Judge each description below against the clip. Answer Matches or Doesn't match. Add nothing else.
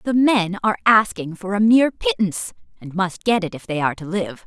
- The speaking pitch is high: Matches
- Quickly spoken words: Matches